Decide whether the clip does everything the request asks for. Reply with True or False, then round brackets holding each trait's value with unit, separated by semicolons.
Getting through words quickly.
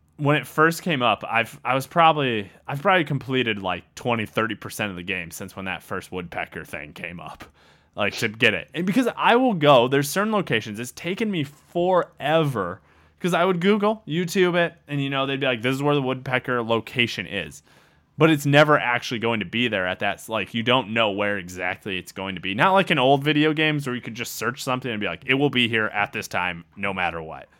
True (230 wpm)